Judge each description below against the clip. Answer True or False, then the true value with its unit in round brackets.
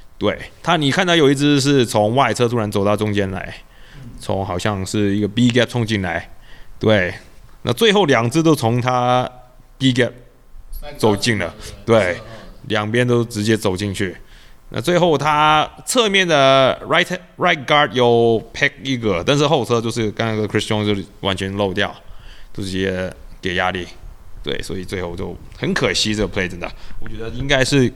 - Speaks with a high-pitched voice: False (110 Hz)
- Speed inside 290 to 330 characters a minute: True (295 characters per minute)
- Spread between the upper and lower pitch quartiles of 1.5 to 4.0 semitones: False (4.8 semitones)